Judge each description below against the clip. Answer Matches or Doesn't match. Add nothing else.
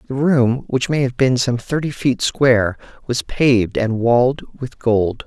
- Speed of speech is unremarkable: Matches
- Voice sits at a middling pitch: Doesn't match